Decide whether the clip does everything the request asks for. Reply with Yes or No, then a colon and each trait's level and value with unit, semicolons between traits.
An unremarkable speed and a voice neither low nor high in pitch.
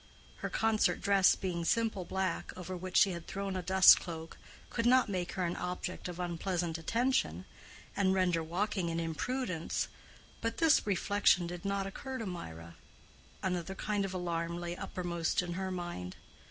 Yes: average, 165 wpm; medium, 180 Hz